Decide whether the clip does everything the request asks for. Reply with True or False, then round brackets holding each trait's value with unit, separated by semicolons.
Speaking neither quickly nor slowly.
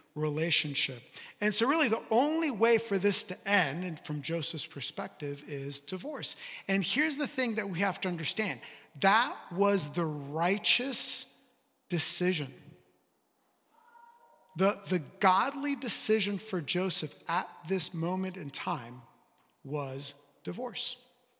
False (125 wpm)